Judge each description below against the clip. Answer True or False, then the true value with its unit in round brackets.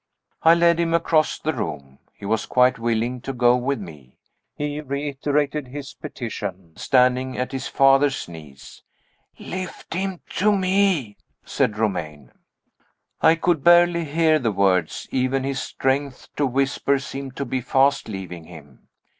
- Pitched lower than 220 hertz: True (135 Hz)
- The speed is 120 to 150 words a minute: True (145 wpm)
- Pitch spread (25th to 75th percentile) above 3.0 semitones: True (5.6 semitones)